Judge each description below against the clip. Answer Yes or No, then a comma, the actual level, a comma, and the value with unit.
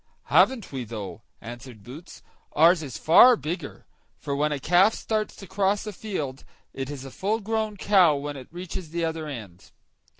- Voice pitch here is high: No, medium, 160 Hz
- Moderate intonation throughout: No, wide, 6.5 semitones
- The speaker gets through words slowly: No, average, 175 wpm